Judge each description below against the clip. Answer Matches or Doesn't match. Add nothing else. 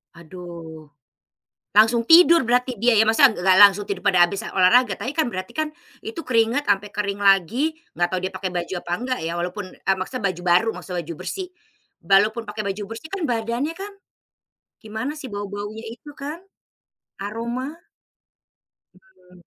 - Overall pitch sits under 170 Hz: Doesn't match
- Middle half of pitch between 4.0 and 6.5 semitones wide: Matches